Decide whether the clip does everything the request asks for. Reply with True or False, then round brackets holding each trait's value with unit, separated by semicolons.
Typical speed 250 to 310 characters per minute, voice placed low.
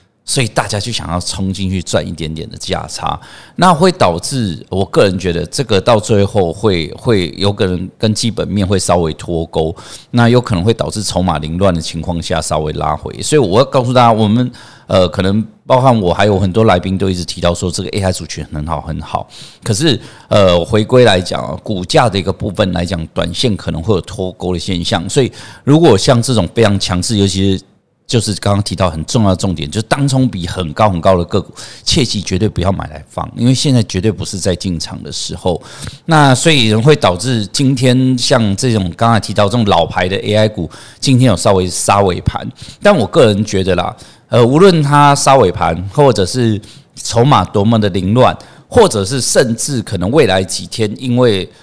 True (300 characters per minute; 100 Hz)